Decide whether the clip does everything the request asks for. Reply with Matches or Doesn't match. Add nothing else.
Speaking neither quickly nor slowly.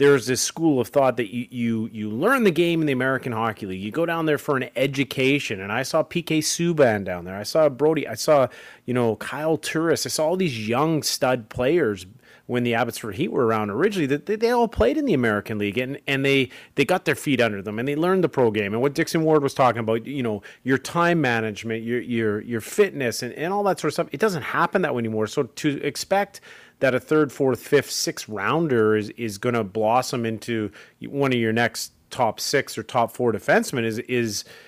Doesn't match